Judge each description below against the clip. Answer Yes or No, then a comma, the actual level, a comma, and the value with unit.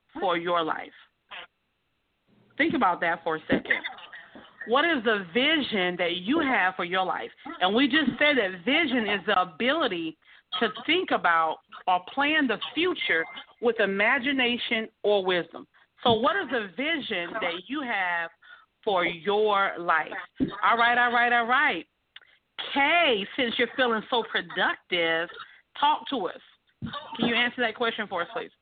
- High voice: Yes, high, 235 Hz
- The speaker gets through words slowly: No, average, 155 wpm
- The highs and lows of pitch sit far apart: Yes, wide, 6.9 semitones